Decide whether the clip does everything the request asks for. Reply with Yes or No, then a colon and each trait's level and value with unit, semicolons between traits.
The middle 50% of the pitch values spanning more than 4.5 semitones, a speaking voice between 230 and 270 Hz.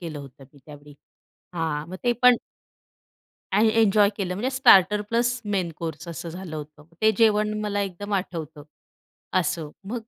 No: average, 5.1 semitones; medium, 185 Hz